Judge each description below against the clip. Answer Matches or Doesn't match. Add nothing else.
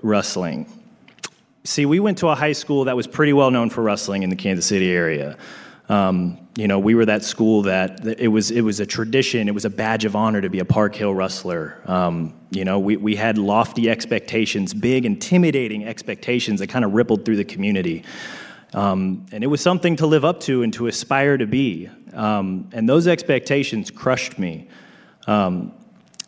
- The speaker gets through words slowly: Doesn't match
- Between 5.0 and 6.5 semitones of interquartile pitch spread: Matches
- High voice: Doesn't match